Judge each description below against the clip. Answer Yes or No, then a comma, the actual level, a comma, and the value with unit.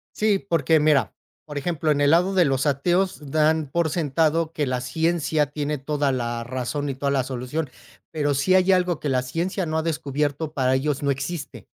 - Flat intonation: No, average, 3.2 semitones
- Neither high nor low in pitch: Yes, medium, 150 Hz